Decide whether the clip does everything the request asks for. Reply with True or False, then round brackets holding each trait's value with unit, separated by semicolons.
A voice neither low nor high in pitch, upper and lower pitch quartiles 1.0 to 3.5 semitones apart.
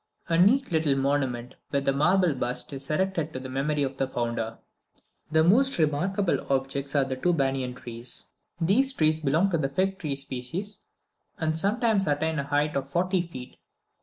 False (150 Hz; 4.8 semitones)